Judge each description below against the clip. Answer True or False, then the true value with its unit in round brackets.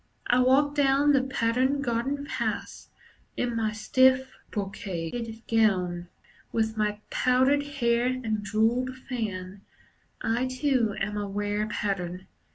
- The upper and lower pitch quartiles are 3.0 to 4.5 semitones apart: True (3.8 semitones)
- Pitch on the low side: False (230 Hz)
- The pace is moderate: False (120 wpm)